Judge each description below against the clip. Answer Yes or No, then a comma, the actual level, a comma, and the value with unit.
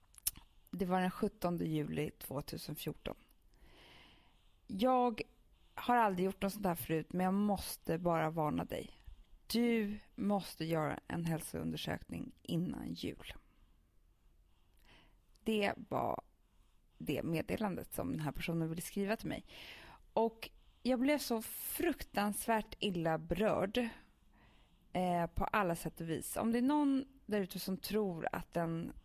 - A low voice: No, medium, 185 Hz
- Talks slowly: Yes, slow, 130 wpm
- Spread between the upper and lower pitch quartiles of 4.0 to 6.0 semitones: Yes, wide, 5.6 semitones